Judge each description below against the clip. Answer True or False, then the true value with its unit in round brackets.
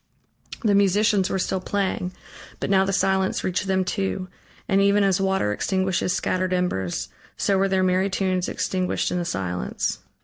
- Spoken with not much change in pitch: True (1.2 semitones)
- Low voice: False (190 Hz)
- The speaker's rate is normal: True (165 wpm)